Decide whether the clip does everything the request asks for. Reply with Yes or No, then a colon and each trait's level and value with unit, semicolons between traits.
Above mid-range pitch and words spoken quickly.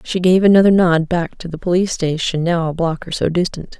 No: medium, 175 Hz; fast, 235 wpm